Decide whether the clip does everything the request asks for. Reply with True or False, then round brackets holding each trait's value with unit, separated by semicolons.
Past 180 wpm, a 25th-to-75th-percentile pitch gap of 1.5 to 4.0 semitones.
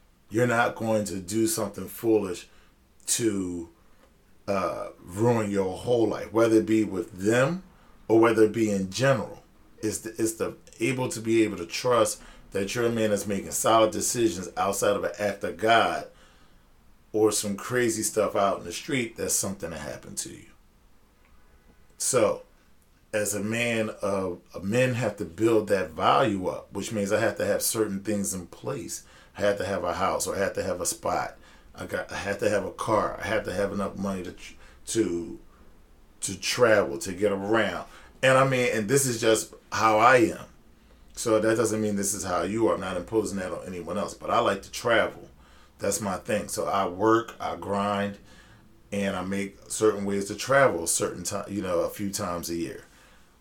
True (195 wpm; 3.2 semitones)